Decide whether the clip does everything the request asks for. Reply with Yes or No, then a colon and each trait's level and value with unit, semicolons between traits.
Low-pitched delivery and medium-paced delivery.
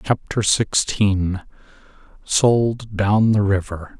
No: low, 105 Hz; slow, 90 wpm